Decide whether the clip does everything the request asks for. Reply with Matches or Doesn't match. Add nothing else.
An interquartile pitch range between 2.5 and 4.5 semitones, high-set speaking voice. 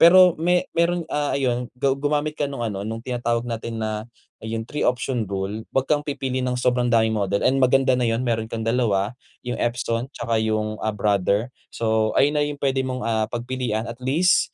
Doesn't match